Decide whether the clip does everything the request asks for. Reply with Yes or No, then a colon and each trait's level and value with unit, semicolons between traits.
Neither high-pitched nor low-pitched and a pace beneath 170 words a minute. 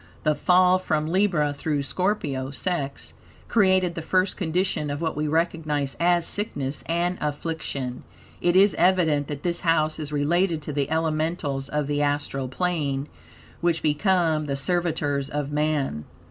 Yes: medium, 155 Hz; average, 145 wpm